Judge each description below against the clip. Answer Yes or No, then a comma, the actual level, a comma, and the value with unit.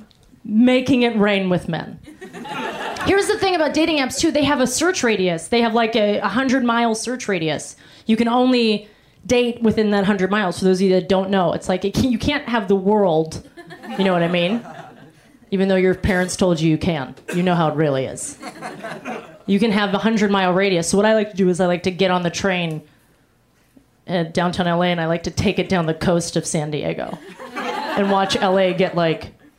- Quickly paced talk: Yes, fast, 220 wpm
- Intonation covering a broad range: No, average, 4.8 semitones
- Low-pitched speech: No, high, 195 Hz